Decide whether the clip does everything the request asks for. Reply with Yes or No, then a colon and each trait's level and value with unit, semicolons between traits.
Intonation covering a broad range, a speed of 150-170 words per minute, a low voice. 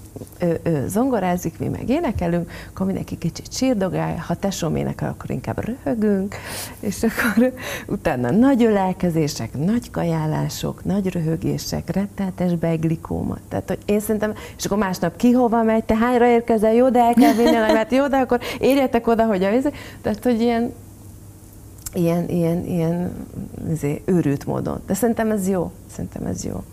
No: wide, 6.1 semitones; fast, 155 wpm; high, 190 Hz